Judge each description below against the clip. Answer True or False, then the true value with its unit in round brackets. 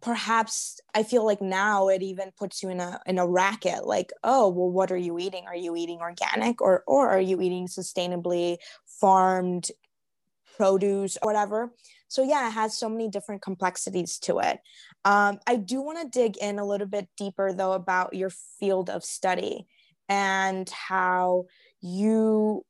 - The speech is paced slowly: False (170 wpm)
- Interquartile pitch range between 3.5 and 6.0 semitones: False (2.8 semitones)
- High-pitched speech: True (195 Hz)